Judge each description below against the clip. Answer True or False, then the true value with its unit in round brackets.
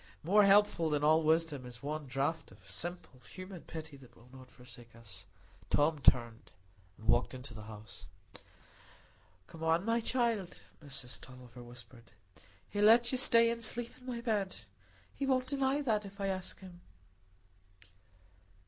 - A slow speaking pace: False (155 wpm)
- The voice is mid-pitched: True (160 Hz)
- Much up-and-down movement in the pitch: True (8.8 semitones)